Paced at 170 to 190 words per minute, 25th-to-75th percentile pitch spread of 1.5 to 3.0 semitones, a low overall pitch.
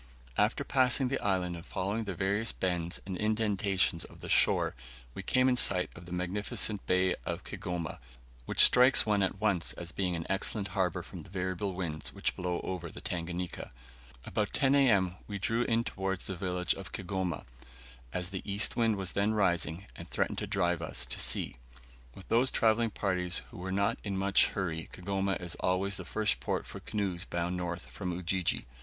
Yes: average, 185 wpm; narrow, 2.5 semitones; very low, 95 Hz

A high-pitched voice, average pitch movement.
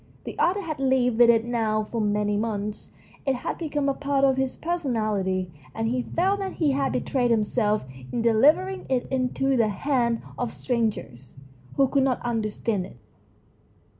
Yes: high, 245 Hz; average, 4.0 semitones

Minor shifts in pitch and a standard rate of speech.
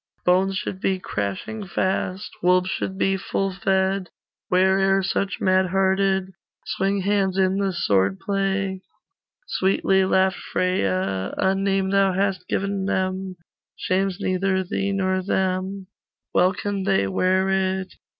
No: narrow, 0.7 semitones; slow, 130 wpm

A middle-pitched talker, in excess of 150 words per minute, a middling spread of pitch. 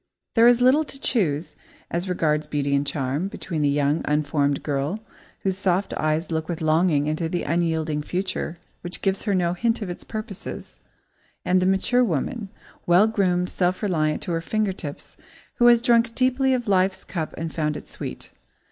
Yes: medium, 175 Hz; average, 180 wpm; average, 4.9 semitones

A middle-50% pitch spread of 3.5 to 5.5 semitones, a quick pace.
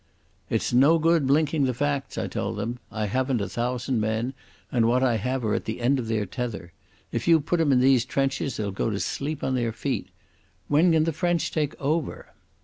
Yes: average, 4.0 semitones; fast, 215 wpm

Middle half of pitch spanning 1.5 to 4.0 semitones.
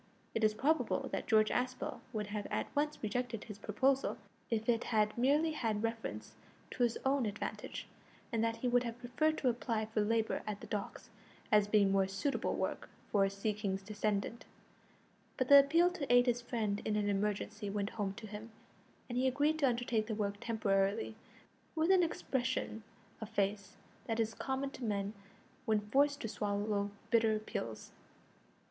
Yes: average, 3.3 semitones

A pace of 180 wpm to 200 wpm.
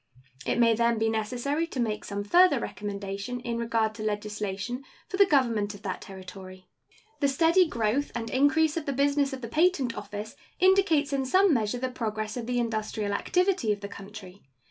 Yes: average, 185 wpm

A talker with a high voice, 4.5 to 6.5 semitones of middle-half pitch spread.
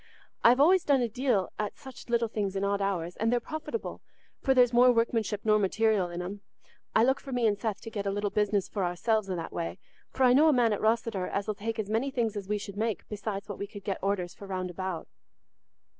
No: high, 215 Hz; average, 3.2 semitones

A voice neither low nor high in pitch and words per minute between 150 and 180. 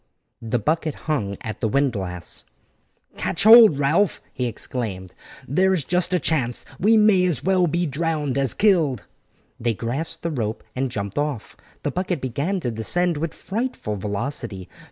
Yes: medium, 145 Hz; average, 160 wpm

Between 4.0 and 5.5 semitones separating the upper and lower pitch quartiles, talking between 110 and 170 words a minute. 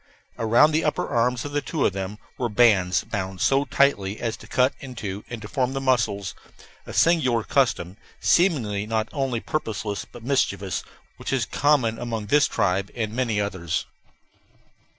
Yes: average, 4.8 semitones; average, 155 wpm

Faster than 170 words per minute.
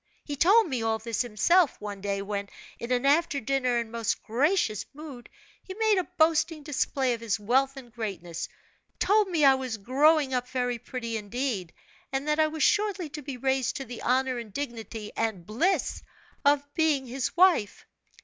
Yes: average, 180 wpm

